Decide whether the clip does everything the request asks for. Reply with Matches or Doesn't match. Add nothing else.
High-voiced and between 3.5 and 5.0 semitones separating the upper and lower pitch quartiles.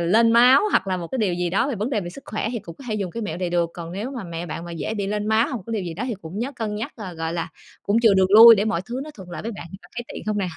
Matches